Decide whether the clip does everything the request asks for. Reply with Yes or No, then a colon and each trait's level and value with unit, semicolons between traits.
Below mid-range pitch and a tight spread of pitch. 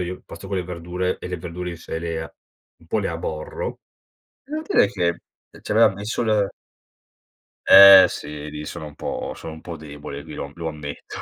No: very low, 85 Hz; average, 3.7 semitones